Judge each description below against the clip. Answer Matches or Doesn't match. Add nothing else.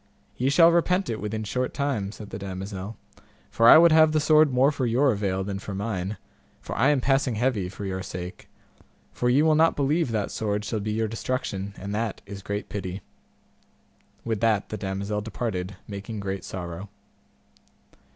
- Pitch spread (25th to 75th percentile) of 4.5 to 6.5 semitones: Matches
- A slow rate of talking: Doesn't match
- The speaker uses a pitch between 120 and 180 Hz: Doesn't match